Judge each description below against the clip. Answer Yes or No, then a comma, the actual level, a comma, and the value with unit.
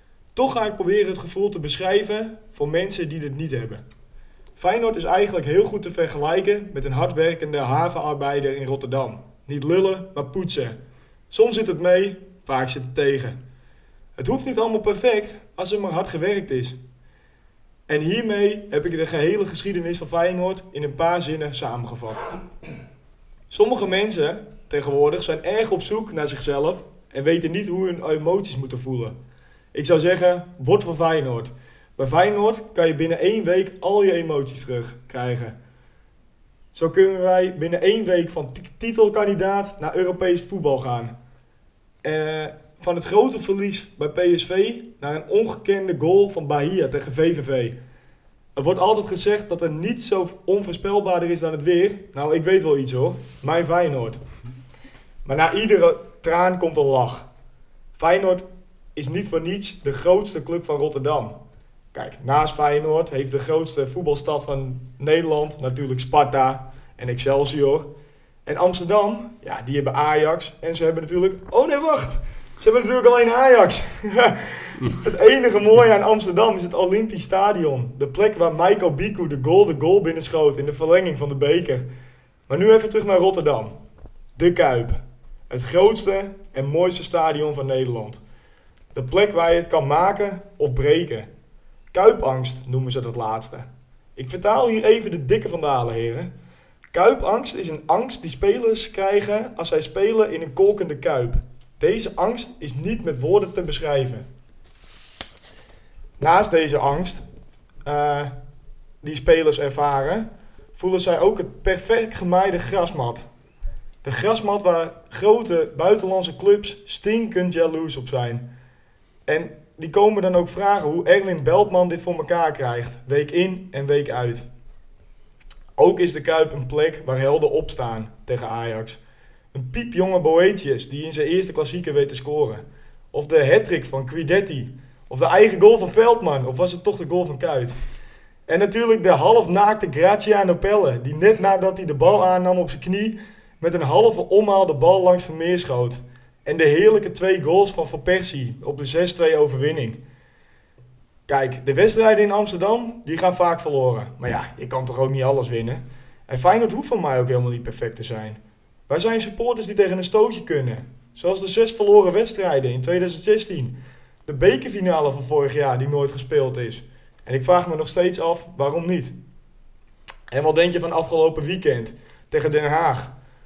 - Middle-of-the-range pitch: Yes, medium, 165 Hz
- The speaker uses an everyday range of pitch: No, wide, 6.5 semitones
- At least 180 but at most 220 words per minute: No, average, 165 wpm